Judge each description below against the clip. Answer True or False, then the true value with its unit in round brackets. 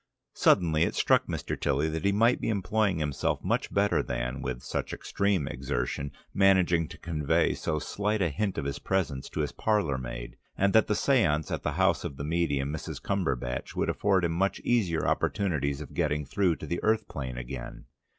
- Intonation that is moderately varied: False (6.1 semitones)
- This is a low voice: True (80 Hz)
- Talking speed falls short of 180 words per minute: False (190 wpm)